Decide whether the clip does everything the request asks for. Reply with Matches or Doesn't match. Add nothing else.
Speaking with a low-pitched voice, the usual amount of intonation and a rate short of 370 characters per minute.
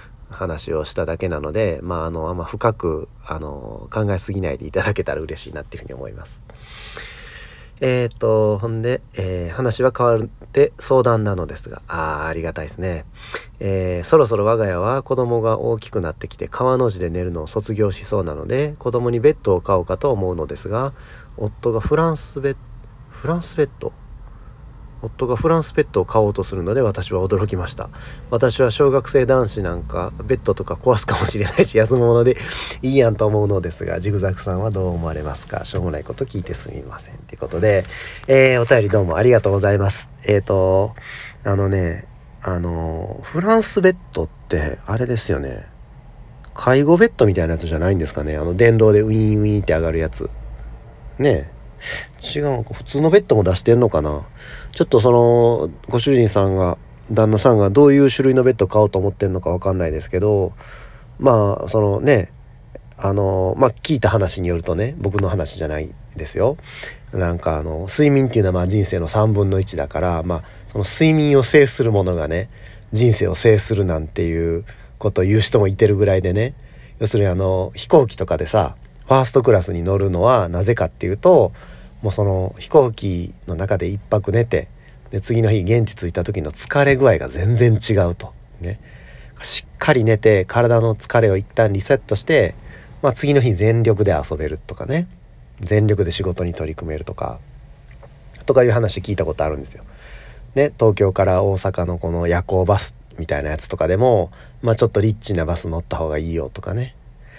Doesn't match